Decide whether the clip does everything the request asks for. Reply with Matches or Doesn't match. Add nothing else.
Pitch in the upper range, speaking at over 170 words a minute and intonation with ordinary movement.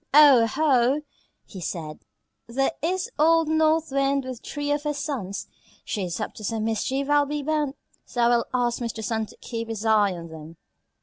Matches